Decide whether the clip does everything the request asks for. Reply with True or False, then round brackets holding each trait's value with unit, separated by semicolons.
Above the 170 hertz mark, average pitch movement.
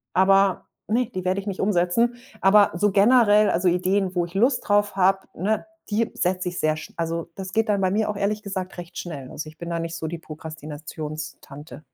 True (185 Hz; 3.5 semitones)